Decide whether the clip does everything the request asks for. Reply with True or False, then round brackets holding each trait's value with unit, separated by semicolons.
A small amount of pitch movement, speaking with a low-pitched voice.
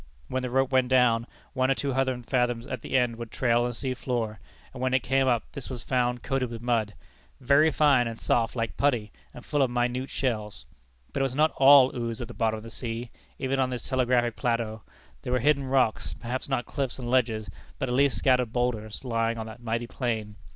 True (2.2 semitones; 125 Hz)